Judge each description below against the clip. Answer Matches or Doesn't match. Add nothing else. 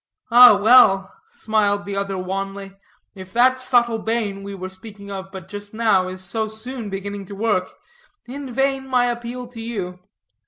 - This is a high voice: Matches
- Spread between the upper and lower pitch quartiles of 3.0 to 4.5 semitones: Matches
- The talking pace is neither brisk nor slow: Matches